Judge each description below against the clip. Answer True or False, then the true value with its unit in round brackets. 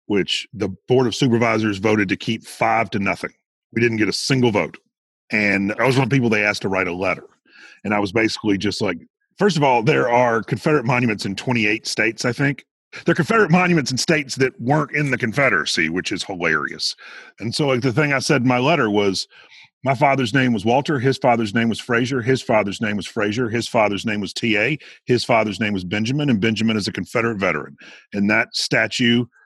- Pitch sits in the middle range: False (120 Hz)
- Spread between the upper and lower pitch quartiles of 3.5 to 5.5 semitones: True (3.8 semitones)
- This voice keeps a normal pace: False (220 wpm)